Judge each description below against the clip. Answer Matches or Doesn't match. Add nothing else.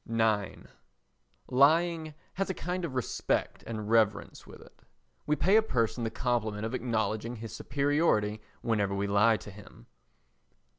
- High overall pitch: Doesn't match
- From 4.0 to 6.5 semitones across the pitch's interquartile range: Matches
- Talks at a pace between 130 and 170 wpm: Matches